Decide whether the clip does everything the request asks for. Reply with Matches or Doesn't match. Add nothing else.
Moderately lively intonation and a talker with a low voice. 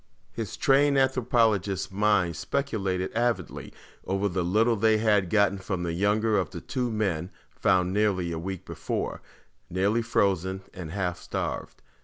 Matches